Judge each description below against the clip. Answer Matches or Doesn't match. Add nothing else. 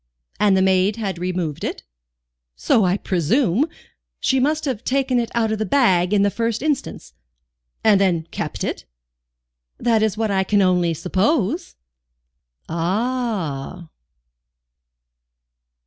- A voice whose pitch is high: Matches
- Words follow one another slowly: Matches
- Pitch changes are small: Doesn't match